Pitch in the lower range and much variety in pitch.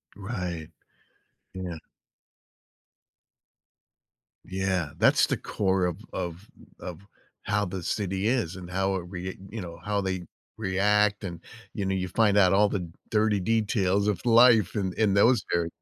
No: very low, 95 Hz; narrow, 2.4 semitones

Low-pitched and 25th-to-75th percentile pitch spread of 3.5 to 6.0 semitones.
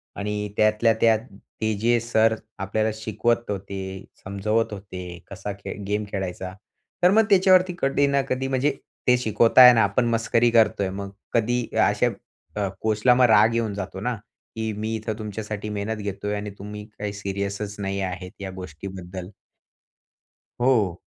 No: low, 105 Hz; average, 2.7 semitones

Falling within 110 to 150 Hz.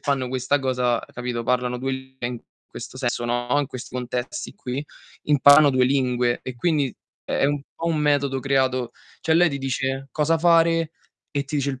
Yes: low, 135 Hz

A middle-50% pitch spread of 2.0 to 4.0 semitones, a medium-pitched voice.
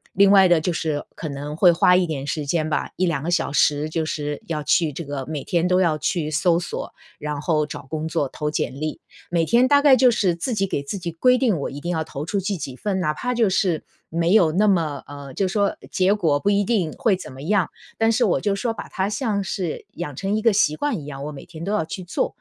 No: average, 4.7 semitones; medium, 170 Hz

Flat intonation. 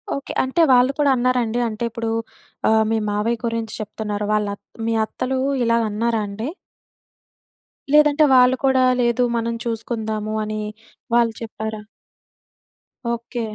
Yes: narrow, 2.3 semitones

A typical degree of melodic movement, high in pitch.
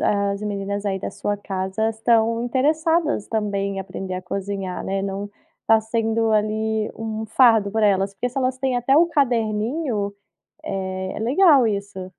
Yes: average, 3.0 semitones; high, 215 Hz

